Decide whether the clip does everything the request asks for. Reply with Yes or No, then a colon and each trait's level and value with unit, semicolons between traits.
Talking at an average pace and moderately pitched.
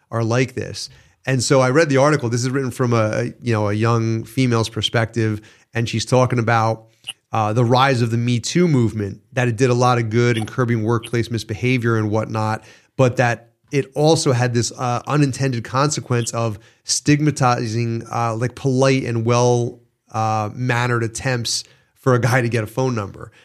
No: average, 185 wpm; low, 120 Hz